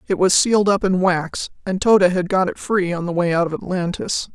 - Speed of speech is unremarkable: No, fast, 250 wpm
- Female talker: Yes, female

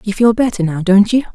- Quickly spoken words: Yes, fast, 270 wpm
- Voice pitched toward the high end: Yes, high, 210 Hz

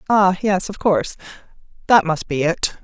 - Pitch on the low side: No, medium, 185 Hz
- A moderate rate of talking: Yes, average, 170 wpm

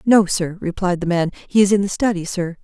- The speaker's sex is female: Yes, female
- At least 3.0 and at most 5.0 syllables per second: No, 5.4 syllables/s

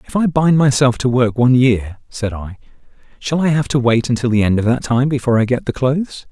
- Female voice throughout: No, male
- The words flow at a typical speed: No, fast, 245 wpm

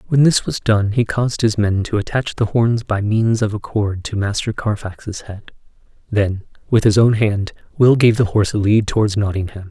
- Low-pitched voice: Yes, low, 105 Hz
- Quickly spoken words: Yes, fast, 210 wpm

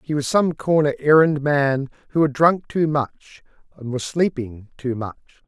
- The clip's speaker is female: No, male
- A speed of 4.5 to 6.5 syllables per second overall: No, 4.3 syllables/s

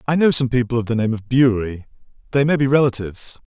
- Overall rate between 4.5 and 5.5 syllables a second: No, 6.9 syllables/s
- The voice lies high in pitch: No, low, 125 Hz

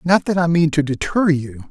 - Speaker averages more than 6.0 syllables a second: No, 5.0 syllables/s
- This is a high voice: No, medium, 160 Hz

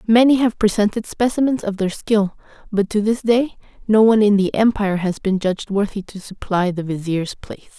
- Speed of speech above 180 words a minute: Yes, average, 195 wpm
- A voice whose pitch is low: No, high, 205 Hz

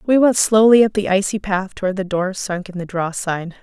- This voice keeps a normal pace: No, fast, 230 wpm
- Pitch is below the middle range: No, high, 195 Hz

